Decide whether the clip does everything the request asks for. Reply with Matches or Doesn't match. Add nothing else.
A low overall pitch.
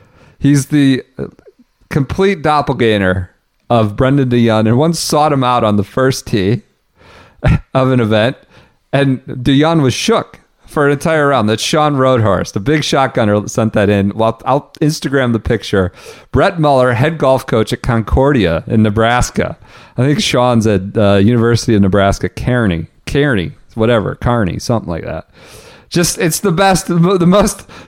Matches